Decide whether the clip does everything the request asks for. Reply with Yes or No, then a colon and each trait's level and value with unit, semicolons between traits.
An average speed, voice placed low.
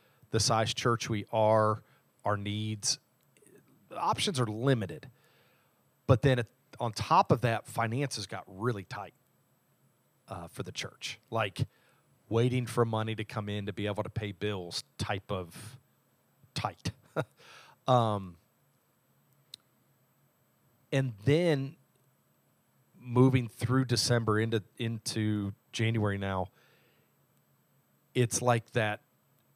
No: slow, 110 wpm; low, 115 Hz